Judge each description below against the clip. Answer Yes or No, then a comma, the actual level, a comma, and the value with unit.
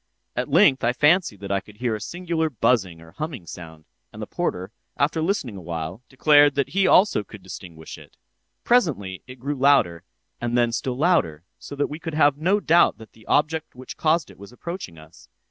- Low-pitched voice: Yes, low, 125 Hz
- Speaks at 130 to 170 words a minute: No, average, 195 wpm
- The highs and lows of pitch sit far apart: Yes, wide, 8.6 semitones